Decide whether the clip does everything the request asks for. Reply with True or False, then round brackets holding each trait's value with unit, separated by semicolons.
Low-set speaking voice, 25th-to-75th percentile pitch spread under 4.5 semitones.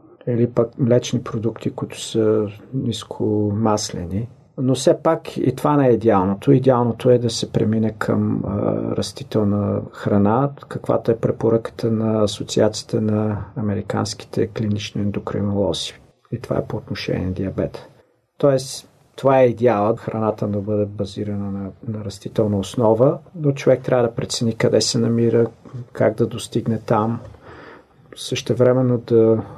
True (115 Hz; 2.9 semitones)